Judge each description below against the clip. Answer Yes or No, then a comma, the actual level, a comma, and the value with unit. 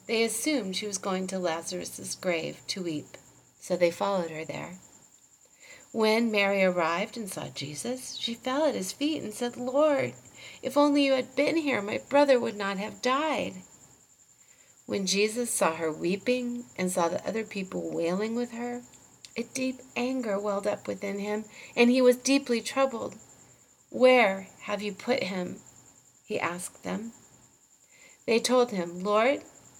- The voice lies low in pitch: No, high, 220 Hz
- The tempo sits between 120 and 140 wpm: No, average, 155 wpm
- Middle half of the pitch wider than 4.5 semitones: Yes, average, 5.2 semitones